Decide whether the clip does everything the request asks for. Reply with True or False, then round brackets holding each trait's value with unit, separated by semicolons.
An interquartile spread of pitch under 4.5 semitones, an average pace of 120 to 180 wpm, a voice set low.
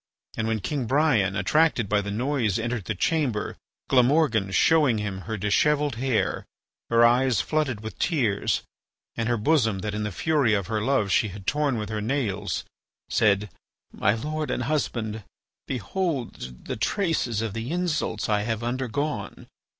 False (5.4 semitones; 160 wpm; 115 Hz)